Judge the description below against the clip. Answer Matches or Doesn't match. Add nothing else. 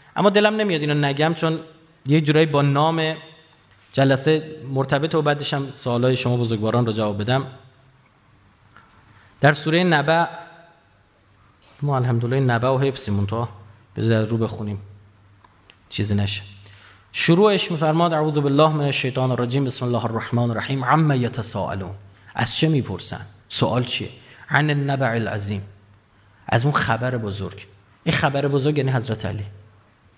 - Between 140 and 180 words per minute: Doesn't match